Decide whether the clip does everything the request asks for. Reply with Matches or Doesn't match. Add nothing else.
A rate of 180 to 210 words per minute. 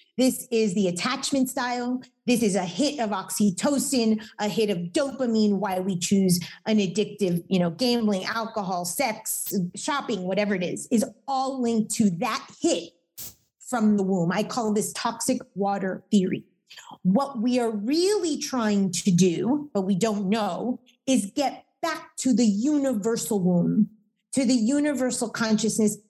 Doesn't match